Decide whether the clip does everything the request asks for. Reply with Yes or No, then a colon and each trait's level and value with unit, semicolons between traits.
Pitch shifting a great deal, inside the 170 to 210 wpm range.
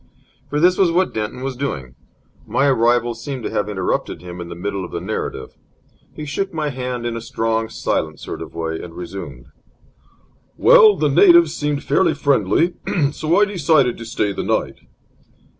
Yes: wide, 7.5 semitones; average, 175 wpm